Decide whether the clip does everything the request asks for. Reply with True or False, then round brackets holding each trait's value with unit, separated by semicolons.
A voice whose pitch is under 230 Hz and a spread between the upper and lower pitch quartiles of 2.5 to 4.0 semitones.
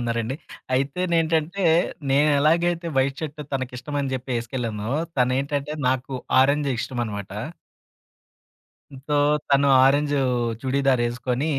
True (135 Hz; 3.0 semitones)